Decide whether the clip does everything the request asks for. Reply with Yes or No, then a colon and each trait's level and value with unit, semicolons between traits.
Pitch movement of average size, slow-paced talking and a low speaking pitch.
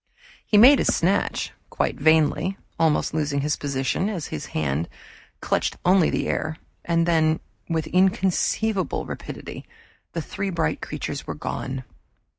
No: average, 4.5 semitones; slow, 130 wpm; medium, 165 Hz